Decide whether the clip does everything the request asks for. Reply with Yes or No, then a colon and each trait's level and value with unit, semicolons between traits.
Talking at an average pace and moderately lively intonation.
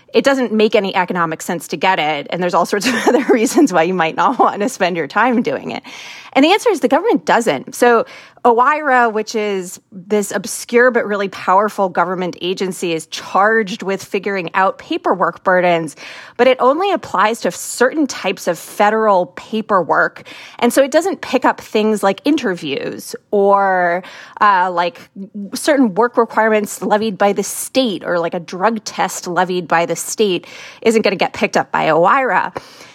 Yes: average, 180 wpm; average, 4.8 semitones